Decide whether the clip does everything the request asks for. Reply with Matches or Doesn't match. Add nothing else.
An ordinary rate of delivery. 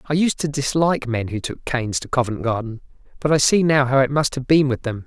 Doesn't match